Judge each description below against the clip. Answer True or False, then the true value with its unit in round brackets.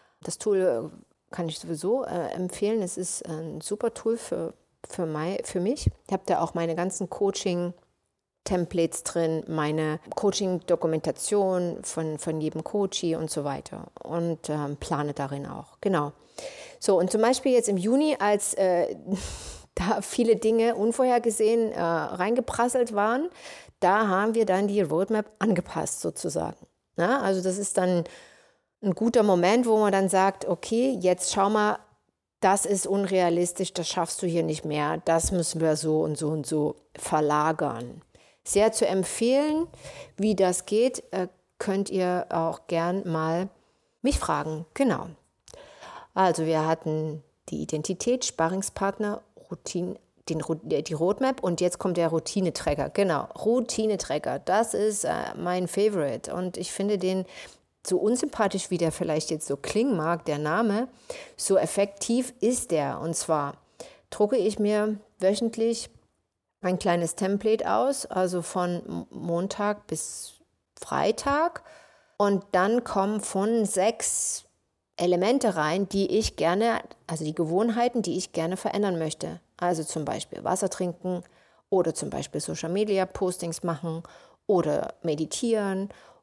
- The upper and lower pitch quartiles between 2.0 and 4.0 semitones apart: False (4.5 semitones)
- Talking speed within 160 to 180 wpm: False (135 wpm)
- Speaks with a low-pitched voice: False (185 Hz)